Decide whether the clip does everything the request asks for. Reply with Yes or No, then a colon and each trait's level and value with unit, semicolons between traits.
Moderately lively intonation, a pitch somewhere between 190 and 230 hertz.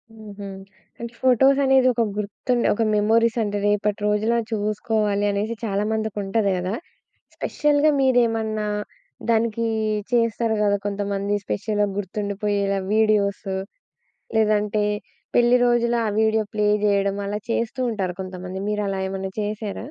No: narrow, 2.2 semitones; high, 210 Hz